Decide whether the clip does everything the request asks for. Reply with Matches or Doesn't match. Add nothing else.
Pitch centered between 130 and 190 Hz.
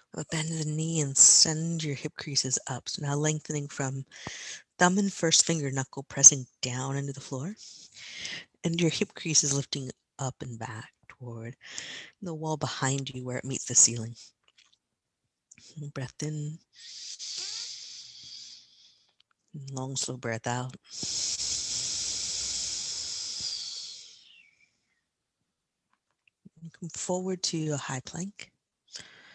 Matches